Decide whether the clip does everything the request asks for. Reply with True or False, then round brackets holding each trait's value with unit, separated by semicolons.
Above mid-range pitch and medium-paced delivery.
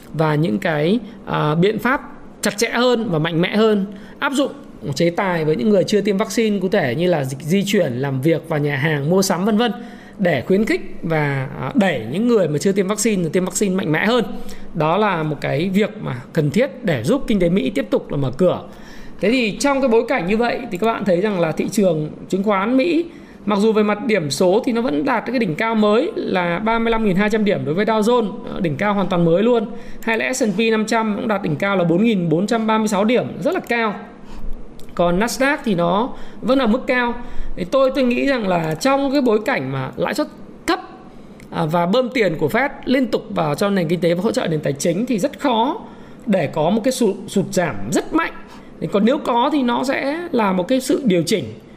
True (220 Hz; 225 wpm)